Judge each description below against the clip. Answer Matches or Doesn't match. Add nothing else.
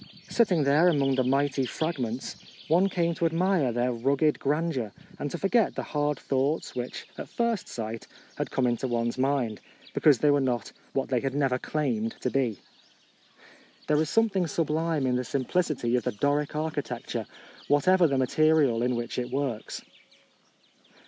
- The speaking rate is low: Doesn't match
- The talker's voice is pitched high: Doesn't match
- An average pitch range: Matches